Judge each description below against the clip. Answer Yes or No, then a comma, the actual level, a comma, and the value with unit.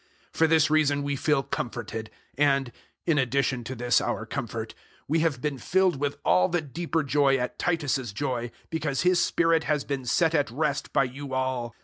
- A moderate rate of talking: Yes, average, 190 wpm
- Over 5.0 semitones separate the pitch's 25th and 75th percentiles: No, average, 3.4 semitones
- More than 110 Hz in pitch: Yes, medium, 140 Hz